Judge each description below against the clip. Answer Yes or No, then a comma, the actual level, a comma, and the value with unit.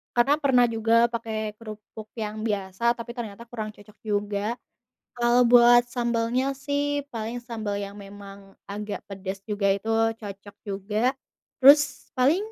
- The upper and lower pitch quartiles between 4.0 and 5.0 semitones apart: No, average, 3.0 semitones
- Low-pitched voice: No, high, 220 Hz